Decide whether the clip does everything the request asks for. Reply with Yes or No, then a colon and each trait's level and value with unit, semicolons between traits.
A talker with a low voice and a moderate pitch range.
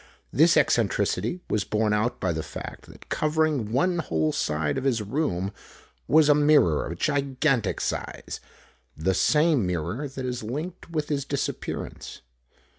No: low, 130 Hz; wide, 6.9 semitones